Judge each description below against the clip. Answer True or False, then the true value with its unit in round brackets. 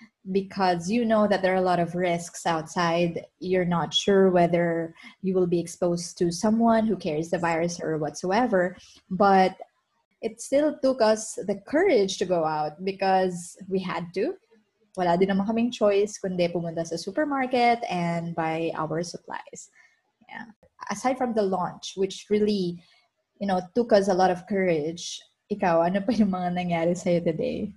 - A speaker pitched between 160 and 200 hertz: True (190 Hz)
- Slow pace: False (155 wpm)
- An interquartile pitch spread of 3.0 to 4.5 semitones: True (3.8 semitones)